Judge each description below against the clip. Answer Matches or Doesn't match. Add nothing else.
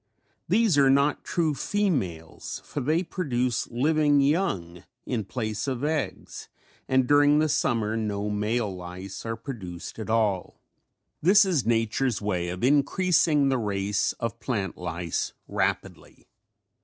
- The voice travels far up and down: Matches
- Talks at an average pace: Doesn't match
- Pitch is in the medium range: Doesn't match